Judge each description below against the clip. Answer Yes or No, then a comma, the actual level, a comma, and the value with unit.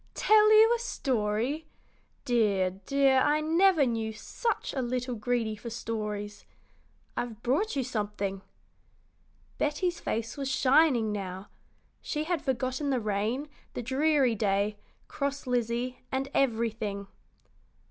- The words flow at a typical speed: No, slow, 120 wpm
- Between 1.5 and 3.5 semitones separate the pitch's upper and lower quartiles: No, average, 4.7 semitones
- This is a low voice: No, high, 245 Hz